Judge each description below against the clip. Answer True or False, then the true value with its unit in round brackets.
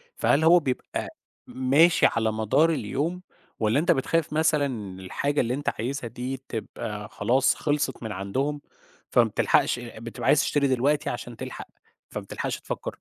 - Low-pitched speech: True (130 Hz)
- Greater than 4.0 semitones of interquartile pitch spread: True (4.8 semitones)